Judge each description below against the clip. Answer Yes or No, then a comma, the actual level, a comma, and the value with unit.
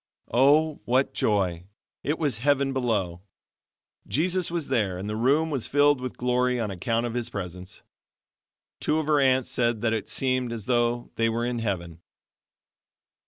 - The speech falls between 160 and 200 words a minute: Yes, average, 165 wpm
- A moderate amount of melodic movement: Yes, average, 4.0 semitones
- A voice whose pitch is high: No, low, 120 Hz